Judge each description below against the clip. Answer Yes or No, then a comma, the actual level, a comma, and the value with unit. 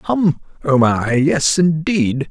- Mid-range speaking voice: Yes, medium, 150 Hz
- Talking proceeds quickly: No, slow, 130 wpm